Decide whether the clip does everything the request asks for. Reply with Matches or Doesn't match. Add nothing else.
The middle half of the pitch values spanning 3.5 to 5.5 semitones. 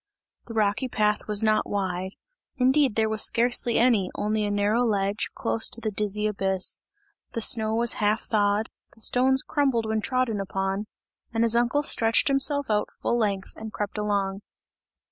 Doesn't match